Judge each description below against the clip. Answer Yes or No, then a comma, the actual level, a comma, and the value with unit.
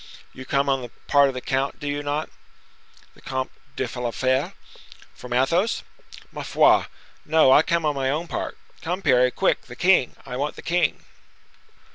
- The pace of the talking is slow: No, average, 175 wpm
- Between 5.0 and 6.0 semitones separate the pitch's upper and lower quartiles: No, average, 3.2 semitones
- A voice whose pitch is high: No, medium, 140 Hz